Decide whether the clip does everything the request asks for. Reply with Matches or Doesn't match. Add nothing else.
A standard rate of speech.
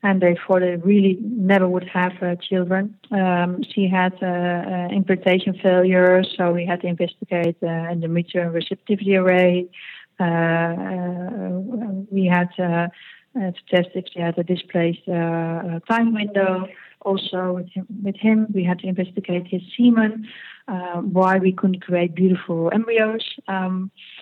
Matches